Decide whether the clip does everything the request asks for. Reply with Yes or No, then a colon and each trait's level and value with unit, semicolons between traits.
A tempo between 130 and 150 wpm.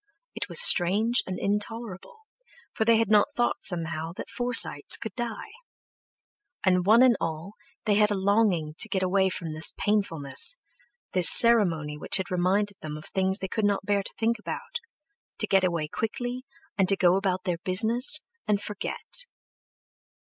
No: average, 160 wpm